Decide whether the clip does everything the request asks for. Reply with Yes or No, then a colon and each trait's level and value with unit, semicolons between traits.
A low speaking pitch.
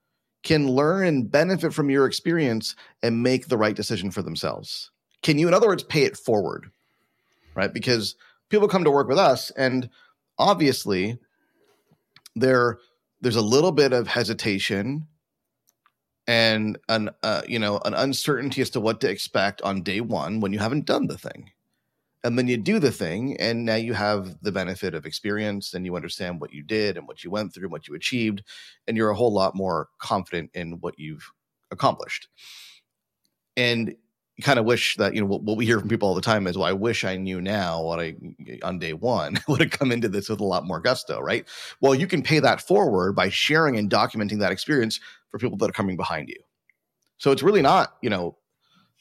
Yes: low, 115 Hz